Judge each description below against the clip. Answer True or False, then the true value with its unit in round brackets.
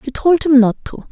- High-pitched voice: True (275 Hz)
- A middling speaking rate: False (270 wpm)